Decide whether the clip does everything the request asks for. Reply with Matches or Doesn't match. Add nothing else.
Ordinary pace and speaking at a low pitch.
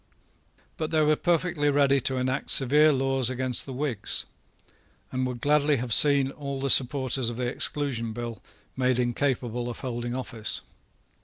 Matches